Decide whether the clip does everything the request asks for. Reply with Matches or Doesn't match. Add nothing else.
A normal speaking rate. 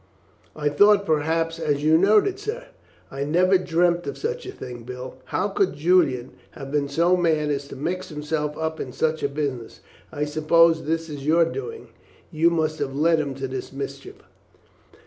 Matches